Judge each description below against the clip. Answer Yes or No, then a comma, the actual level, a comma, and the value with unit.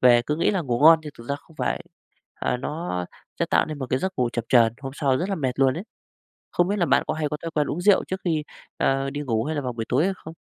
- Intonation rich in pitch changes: No, average, 4.4 semitones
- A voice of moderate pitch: Yes, medium, 145 Hz